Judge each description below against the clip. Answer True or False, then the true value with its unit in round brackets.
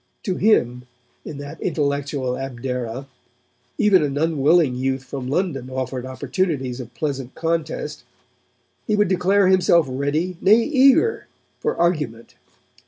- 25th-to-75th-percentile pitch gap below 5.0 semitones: False (5.5 semitones)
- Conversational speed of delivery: False (120 wpm)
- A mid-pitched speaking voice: True (145 Hz)